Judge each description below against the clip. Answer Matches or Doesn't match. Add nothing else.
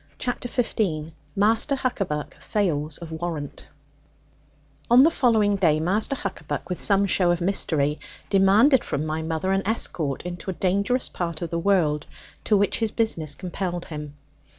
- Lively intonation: Doesn't match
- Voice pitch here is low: Doesn't match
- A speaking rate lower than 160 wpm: Matches